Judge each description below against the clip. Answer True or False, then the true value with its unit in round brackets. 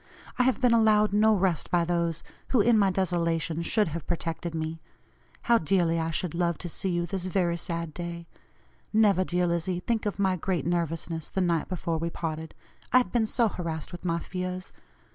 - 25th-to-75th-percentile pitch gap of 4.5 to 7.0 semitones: False (2.7 semitones)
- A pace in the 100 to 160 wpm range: False (195 wpm)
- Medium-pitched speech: True (175 Hz)